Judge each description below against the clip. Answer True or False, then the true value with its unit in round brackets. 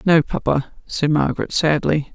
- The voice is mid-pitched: True (155 Hz)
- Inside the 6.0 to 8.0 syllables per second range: False (4.7 syllables/s)